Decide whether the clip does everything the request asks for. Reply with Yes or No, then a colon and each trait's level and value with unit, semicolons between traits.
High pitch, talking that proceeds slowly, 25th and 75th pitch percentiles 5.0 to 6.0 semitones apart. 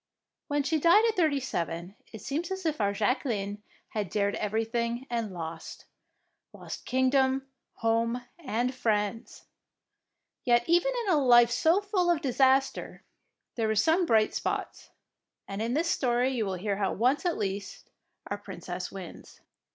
No: high, 240 Hz; average, 155 wpm; wide, 5.6 semitones